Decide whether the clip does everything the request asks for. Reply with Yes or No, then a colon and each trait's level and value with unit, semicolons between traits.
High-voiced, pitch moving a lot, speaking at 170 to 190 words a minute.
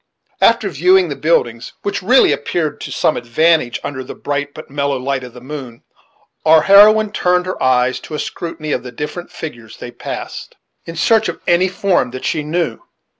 No: medium, 155 Hz; wide, 5.7 semitones; average, 185 wpm